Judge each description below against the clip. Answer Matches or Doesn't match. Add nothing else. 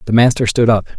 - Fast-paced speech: Matches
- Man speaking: Matches